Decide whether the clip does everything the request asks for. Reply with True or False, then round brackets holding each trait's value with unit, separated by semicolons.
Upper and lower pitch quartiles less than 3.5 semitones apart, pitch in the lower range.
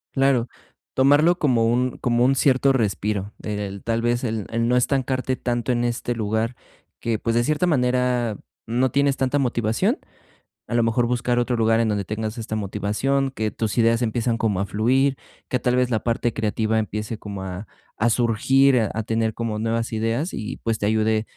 True (2.5 semitones; 115 Hz)